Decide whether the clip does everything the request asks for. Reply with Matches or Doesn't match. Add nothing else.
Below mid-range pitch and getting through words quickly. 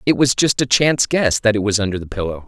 Matches